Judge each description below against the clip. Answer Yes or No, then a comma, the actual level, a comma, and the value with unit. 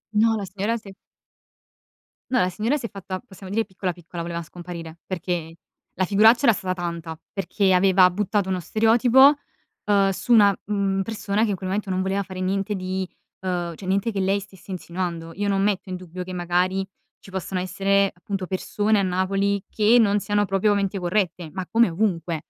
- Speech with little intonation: Yes, narrow, 2.2 semitones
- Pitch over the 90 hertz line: Yes, high, 190 Hz